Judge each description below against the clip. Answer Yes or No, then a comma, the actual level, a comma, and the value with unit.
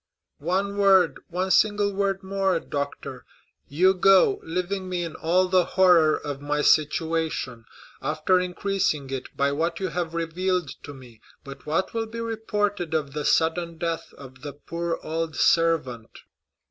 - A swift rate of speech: No, average, 145 wpm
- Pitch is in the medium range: Yes, medium, 170 Hz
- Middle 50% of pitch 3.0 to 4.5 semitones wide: Yes, average, 3.9 semitones